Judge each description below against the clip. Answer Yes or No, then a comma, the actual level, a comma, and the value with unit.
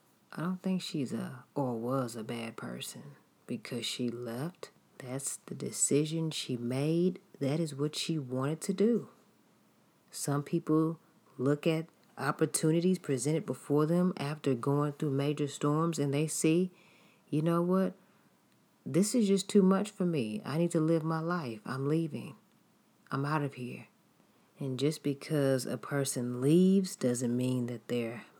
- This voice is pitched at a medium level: Yes, medium, 150 Hz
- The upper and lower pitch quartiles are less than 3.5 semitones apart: No, average, 4.2 semitones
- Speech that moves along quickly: No, average, 155 wpm